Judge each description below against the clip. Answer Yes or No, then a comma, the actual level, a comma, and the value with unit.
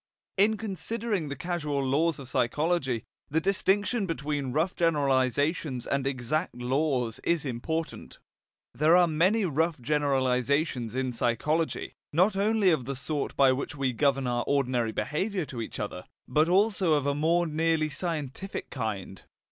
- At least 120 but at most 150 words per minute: Yes, average, 145 wpm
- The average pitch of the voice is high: No, medium, 150 Hz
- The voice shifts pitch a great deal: No, average, 4.6 semitones